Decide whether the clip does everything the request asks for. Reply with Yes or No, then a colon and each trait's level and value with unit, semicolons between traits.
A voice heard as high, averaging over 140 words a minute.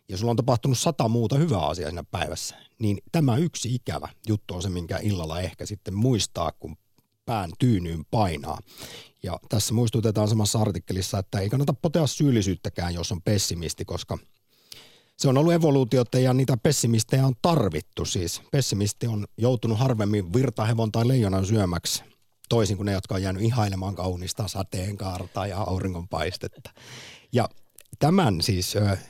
No: low, 110 Hz; average, 150 wpm